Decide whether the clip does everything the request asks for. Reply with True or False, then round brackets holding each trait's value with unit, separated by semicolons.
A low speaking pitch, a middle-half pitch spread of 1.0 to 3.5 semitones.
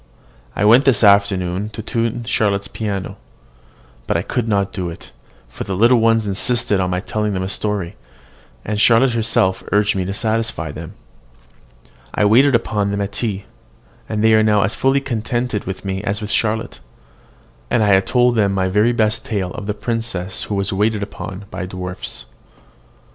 True (105 Hz; 2.7 semitones)